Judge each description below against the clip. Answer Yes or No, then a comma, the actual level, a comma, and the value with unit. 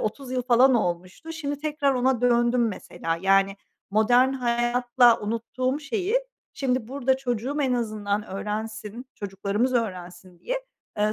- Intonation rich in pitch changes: No, average, 3.8 semitones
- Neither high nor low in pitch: No, high, 240 Hz